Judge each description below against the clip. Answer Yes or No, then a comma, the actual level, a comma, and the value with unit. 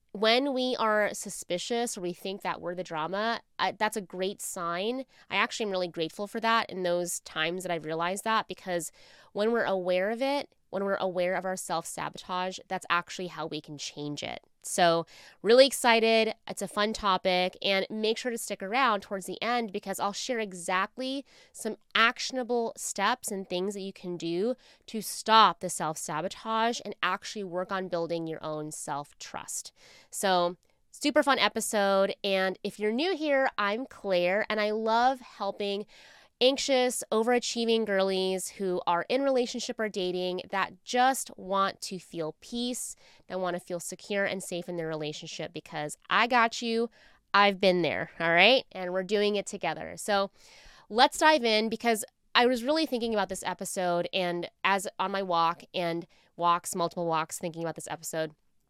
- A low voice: No, high, 195 Hz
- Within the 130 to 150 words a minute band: No, average, 175 wpm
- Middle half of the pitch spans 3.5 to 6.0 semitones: Yes, average, 4.2 semitones